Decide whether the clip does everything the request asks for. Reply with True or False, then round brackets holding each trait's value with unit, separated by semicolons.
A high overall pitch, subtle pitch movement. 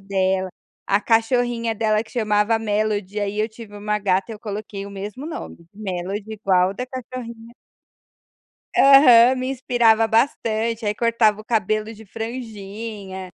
True (215 Hz; 2.3 semitones)